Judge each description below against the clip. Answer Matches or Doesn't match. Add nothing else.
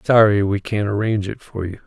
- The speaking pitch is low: Matches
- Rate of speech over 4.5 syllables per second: Matches